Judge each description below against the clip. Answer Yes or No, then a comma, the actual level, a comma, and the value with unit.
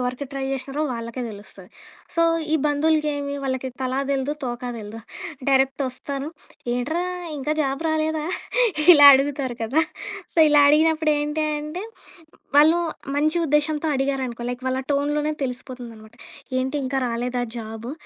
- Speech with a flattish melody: No, average, 3.3 semitones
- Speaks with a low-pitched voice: No, very high, 275 Hz